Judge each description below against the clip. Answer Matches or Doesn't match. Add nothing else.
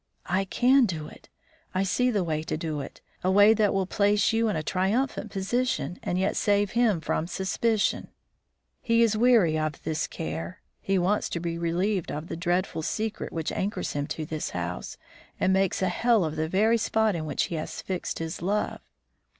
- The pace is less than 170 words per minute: Doesn't match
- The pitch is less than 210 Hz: Matches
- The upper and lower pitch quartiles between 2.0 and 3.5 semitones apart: Doesn't match